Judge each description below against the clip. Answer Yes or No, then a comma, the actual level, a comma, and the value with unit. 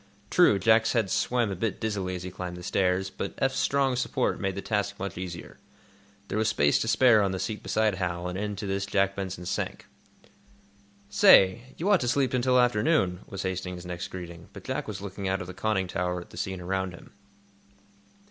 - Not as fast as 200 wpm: No, fast, 205 wpm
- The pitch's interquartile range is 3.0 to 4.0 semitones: Yes, average, 3.3 semitones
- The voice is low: Yes, very low, 95 Hz